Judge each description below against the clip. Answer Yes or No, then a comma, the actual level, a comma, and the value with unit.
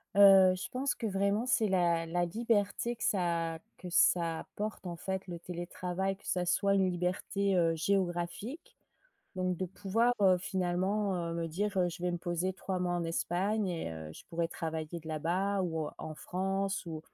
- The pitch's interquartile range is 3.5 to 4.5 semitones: No, narrow, 2.5 semitones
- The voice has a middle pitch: Yes, medium, 180 Hz